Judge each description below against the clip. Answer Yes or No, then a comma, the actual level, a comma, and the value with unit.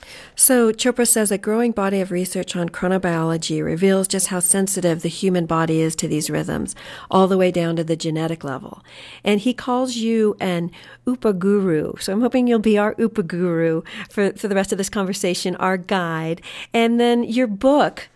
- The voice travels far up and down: No, average, 4.2 semitones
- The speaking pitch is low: No, high, 190 Hz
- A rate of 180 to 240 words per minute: Yes, average, 190 wpm